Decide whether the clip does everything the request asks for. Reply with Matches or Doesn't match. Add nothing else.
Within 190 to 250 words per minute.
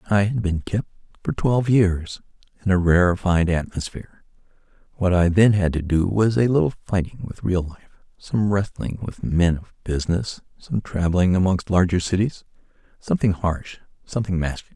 Doesn't match